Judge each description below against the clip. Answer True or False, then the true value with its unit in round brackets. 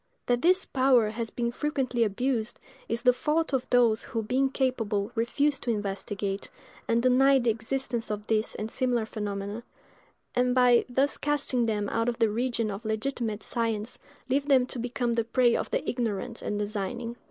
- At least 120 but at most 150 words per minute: False (175 wpm)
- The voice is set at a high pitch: True (235 Hz)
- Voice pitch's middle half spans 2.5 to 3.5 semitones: True (2.8 semitones)